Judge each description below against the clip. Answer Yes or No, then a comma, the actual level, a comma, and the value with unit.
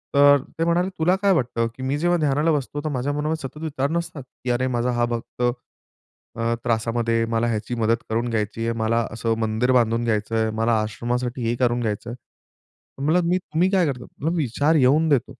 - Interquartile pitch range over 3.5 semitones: Yes, average, 4.3 semitones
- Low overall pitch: Yes, low, 125 Hz